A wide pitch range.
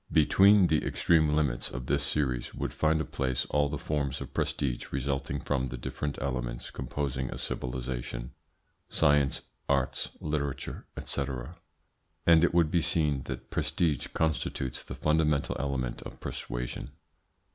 No: average, 3.3 semitones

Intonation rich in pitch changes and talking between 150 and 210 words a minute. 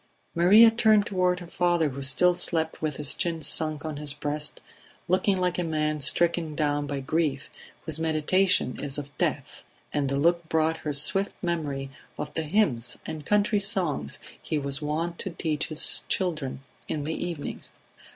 No: average, 3.2 semitones; average, 170 wpm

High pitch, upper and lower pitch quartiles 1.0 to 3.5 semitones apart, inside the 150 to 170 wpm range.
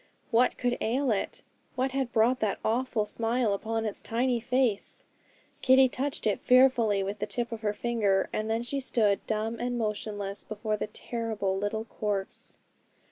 Yes: high, 225 Hz; average, 2.8 semitones; average, 165 wpm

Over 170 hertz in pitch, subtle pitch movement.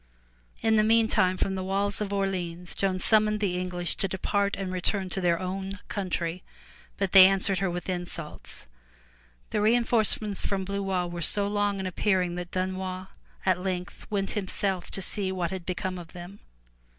Yes: high, 190 Hz; narrow, 1.8 semitones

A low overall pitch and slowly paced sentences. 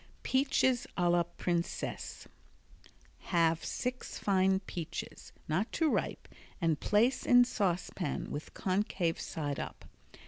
No: medium, 185 Hz; slow, 110 wpm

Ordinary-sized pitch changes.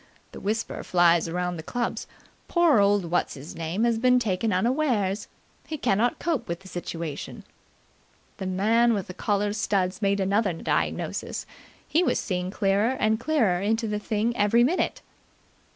Yes: average, 4.2 semitones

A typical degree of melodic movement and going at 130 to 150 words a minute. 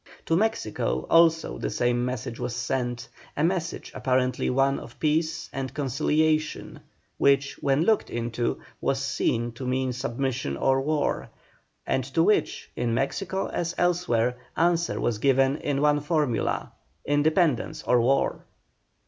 Yes: average, 4.2 semitones; slow, 135 wpm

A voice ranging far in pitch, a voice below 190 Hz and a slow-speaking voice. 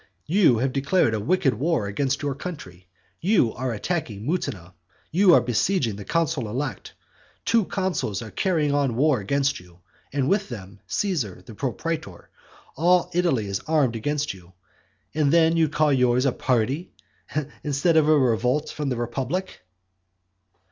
No: wide, 6.1 semitones; medium, 140 Hz; average, 155 wpm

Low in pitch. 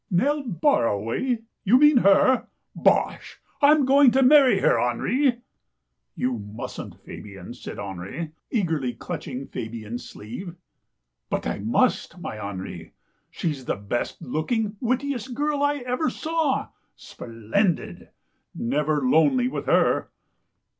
No: medium, 170 Hz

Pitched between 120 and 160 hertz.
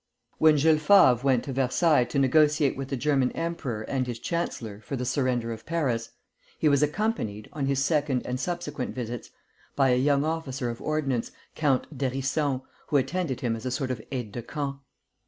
Yes: low, 135 Hz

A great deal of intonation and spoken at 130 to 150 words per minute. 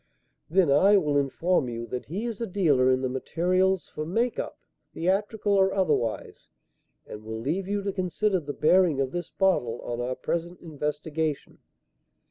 No: wide, 5.7 semitones; average, 165 wpm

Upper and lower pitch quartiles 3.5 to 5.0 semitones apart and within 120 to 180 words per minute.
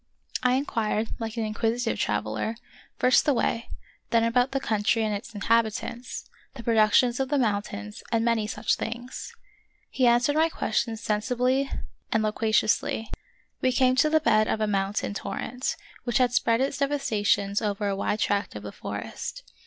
No: average, 3.0 semitones; average, 165 wpm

